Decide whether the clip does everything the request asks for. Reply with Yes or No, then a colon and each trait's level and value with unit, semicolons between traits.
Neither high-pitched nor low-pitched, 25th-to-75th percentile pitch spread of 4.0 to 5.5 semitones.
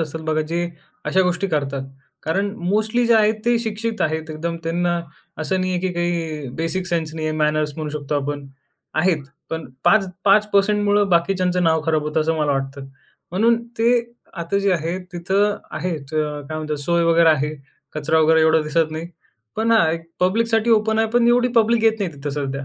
Yes: medium, 170 Hz; average, 4.7 semitones